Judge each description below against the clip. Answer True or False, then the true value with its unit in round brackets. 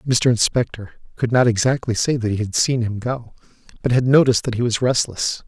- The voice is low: True (120 Hz)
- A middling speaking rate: False (210 wpm)